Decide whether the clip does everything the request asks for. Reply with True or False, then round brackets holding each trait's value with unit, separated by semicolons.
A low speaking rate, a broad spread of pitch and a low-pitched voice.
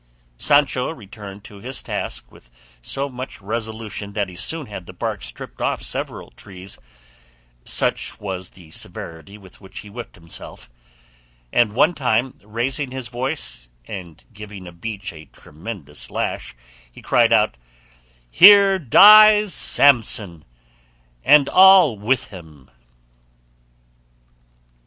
True (125 wpm; 6.1 semitones; 105 Hz)